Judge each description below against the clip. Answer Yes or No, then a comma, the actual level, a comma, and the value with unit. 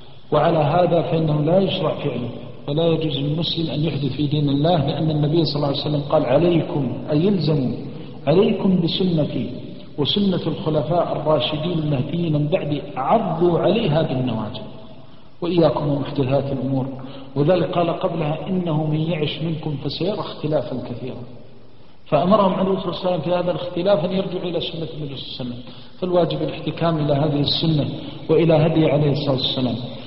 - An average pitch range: Yes, average, 3.4 semitones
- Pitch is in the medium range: Yes, medium, 155 Hz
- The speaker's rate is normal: No, fast, 150 wpm